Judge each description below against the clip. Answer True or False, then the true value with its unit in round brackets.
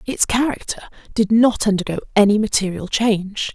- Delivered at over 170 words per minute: False (135 wpm)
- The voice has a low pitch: False (210 Hz)